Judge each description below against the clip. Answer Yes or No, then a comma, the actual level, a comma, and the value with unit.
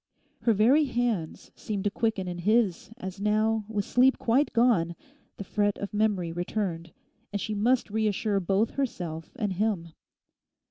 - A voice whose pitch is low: No, high, 210 Hz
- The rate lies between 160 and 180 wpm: No, average, 150 wpm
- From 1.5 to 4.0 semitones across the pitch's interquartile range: Yes, average, 3.1 semitones